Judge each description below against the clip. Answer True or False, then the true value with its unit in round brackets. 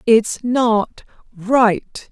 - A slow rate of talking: True (85 wpm)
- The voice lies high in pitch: True (225 Hz)